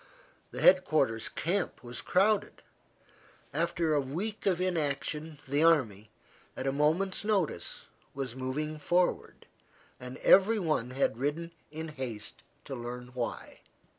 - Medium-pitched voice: Yes, medium, 150 Hz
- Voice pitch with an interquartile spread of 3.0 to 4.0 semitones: No, average, 5.0 semitones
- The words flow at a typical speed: No, slow, 130 wpm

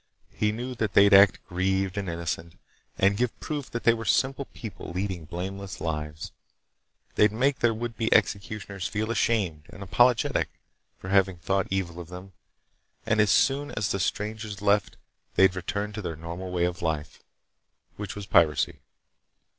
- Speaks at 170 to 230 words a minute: No, average, 160 wpm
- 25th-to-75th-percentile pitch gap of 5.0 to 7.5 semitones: No, average, 3.5 semitones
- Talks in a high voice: No, low, 100 Hz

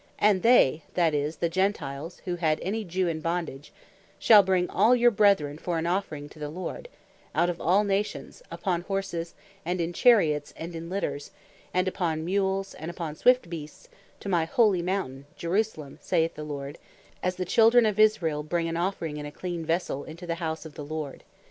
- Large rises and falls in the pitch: No, average, 3.7 semitones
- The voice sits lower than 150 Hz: No, medium, 175 Hz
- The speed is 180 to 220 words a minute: Yes, average, 190 wpm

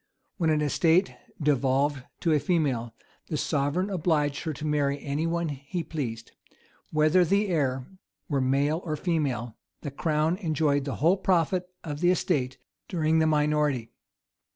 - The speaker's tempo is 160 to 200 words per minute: No, average, 145 wpm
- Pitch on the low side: No, medium, 150 Hz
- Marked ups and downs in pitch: No, average, 3.0 semitones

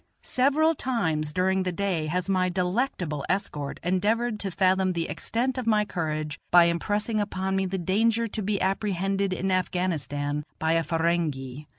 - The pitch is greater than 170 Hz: Yes, medium, 185 Hz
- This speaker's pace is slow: No, average, 160 wpm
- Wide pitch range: No, average, 3.8 semitones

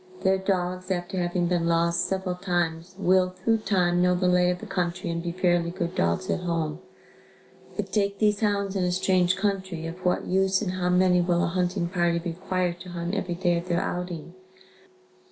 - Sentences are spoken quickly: No, average, 195 wpm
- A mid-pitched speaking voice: Yes, medium, 180 Hz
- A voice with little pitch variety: Yes, narrow, 1.5 semitones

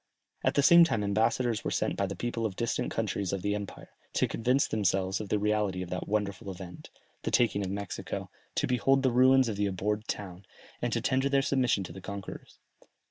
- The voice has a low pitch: Yes, low, 105 Hz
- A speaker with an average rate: No, fast, 215 wpm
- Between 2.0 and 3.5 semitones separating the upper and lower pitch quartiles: No, average, 3.9 semitones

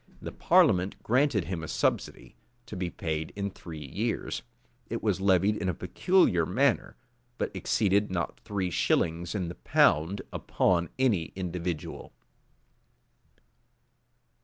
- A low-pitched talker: Yes, very low, 90 Hz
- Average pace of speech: No, slow, 125 wpm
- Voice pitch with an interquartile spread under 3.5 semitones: Yes, average, 3.1 semitones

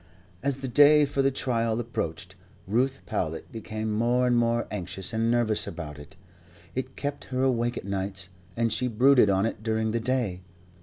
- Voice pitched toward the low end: Yes, low, 115 Hz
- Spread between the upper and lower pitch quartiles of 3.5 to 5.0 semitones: Yes, average, 3.8 semitones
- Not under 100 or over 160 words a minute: No, average, 175 wpm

